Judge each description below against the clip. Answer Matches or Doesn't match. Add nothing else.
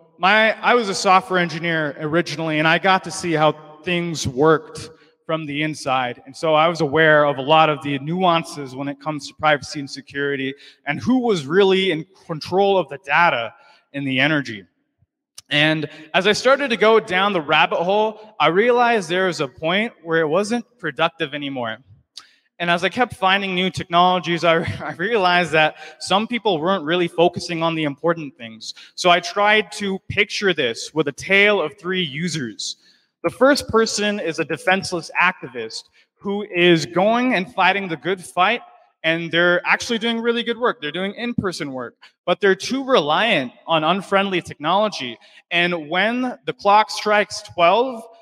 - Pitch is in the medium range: Matches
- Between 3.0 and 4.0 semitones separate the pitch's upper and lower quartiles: Doesn't match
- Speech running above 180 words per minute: Doesn't match